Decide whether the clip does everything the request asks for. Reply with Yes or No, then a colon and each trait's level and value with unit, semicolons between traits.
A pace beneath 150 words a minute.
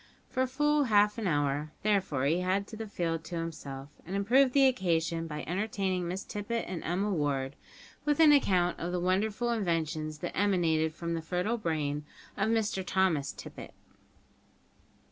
No: average, 160 wpm